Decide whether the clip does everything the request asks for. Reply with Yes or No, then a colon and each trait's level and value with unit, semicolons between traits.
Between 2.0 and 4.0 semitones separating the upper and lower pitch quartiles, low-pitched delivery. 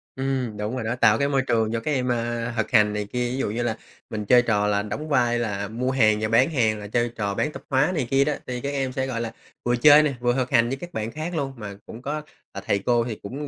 Yes: average, 3.6 semitones; low, 120 Hz